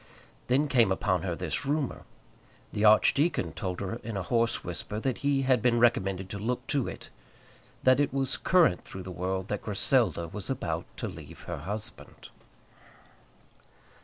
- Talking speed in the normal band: Yes, average, 160 wpm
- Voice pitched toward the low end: Yes, low, 110 Hz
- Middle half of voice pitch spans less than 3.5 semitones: No, wide, 5.6 semitones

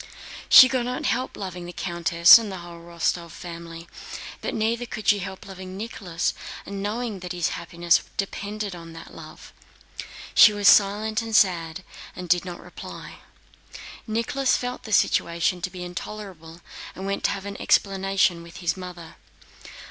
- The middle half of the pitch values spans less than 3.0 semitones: No, average, 3.5 semitones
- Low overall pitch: No, high, 190 Hz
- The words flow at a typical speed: Yes, average, 160 wpm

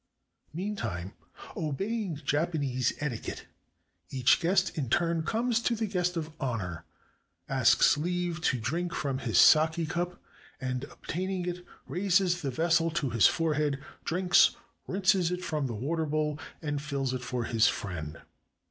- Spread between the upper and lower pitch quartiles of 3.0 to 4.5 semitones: No, average, 5.1 semitones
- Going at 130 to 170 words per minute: Yes, average, 140 wpm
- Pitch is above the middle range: No, medium, 160 Hz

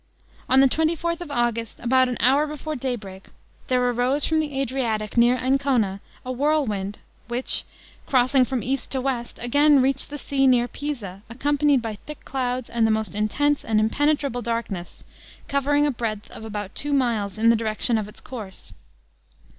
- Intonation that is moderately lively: Yes, average, 4.0 semitones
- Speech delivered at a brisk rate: No, average, 170 wpm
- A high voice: Yes, very high, 250 Hz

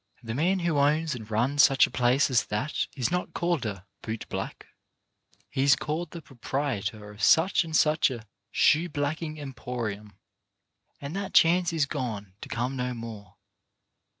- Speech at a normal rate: Yes, average, 165 wpm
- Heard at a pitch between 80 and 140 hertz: Yes, low, 135 Hz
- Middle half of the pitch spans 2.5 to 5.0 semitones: No, wide, 5.4 semitones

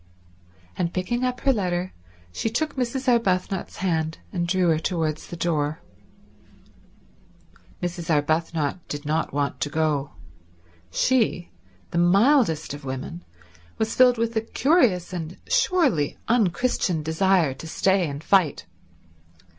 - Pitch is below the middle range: No, medium, 175 Hz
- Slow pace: Yes, slow, 125 wpm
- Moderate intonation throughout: No, wide, 6.2 semitones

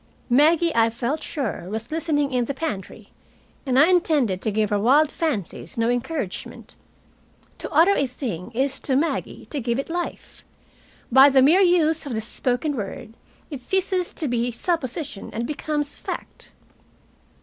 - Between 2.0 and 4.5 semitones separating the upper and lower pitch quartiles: No, average, 5.2 semitones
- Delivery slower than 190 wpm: Yes, average, 160 wpm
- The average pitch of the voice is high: Yes, very high, 275 Hz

